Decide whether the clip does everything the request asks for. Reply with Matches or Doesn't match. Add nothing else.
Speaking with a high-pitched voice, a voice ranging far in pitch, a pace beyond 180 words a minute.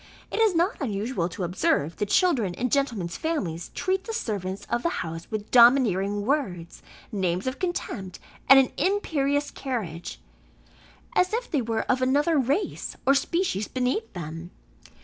Doesn't match